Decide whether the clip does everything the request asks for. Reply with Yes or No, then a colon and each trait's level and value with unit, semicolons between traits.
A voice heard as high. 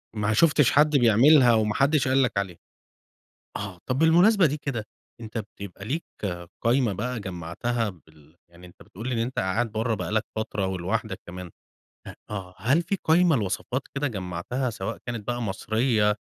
No: low, 115 Hz